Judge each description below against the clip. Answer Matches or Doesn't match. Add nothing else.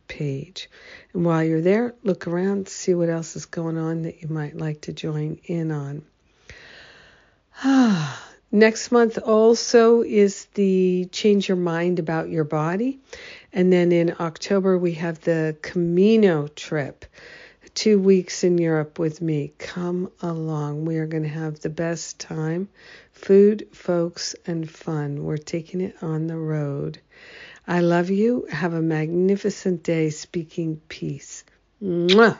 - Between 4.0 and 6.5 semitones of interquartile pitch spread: Doesn't match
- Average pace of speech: Matches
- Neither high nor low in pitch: Matches